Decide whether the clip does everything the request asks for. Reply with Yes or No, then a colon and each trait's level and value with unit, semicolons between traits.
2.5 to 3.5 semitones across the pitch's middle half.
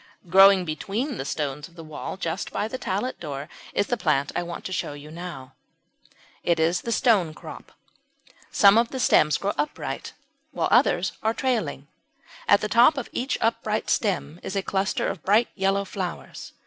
No: wide, 5.4 semitones